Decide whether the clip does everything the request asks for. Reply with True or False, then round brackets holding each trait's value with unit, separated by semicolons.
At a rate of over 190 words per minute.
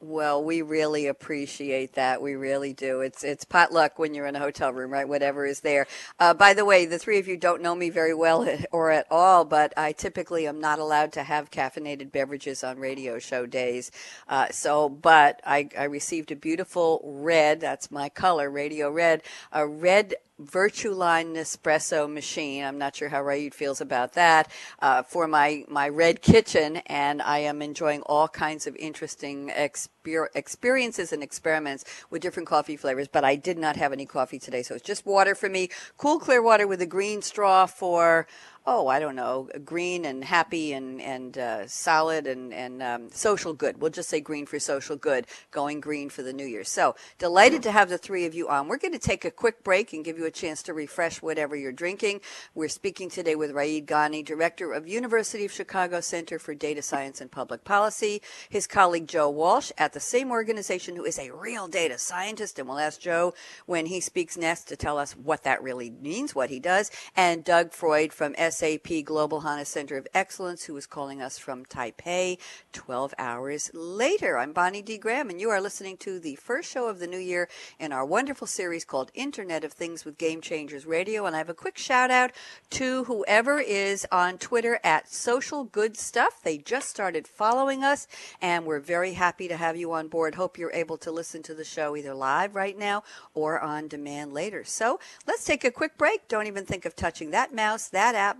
True (205 wpm)